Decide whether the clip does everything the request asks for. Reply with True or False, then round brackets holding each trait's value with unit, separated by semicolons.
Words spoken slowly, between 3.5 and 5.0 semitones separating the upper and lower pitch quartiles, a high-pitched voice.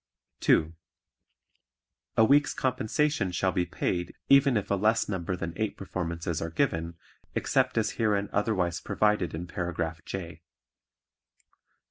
False (125 wpm; 4.2 semitones; 95 Hz)